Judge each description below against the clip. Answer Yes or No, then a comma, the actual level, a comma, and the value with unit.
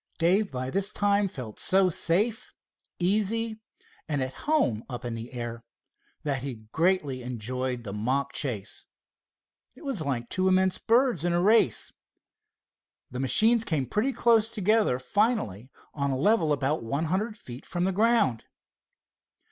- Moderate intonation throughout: No, wide, 8.6 semitones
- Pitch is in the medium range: Yes, medium, 160 Hz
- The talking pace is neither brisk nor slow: Yes, average, 150 wpm